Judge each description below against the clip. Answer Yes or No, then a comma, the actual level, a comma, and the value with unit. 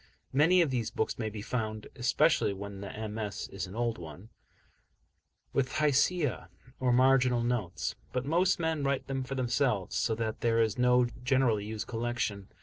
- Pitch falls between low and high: No, low, 120 Hz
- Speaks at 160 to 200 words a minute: Yes, average, 165 wpm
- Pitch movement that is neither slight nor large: Yes, average, 3.6 semitones